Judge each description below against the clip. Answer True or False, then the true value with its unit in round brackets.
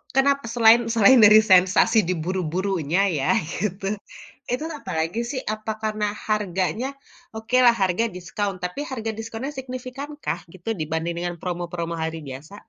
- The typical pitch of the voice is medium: False (205 Hz)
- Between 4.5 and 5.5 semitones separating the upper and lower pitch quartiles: True (4.9 semitones)